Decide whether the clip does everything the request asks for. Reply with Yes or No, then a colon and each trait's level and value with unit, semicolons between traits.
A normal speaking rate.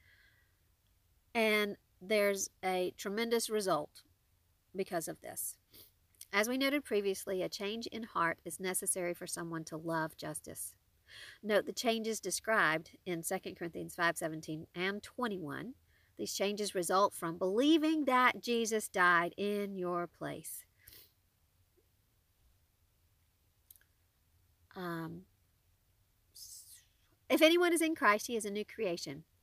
No: slow, 115 wpm